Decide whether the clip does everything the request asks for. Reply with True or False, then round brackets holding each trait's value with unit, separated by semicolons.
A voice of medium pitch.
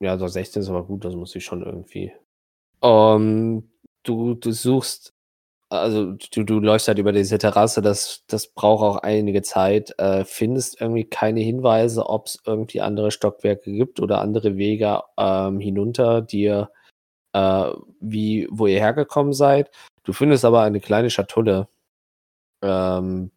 False (105 Hz)